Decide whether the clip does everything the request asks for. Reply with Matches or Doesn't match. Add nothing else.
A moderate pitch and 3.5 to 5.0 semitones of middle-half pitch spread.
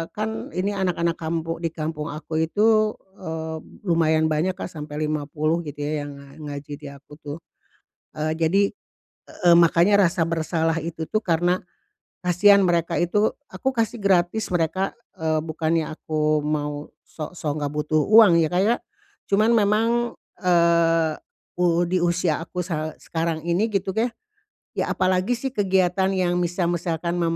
Doesn't match